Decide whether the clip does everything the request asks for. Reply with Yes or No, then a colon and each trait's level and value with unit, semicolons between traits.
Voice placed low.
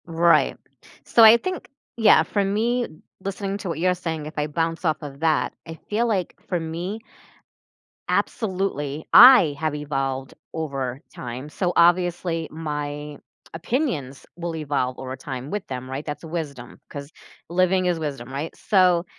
No: medium, 165 Hz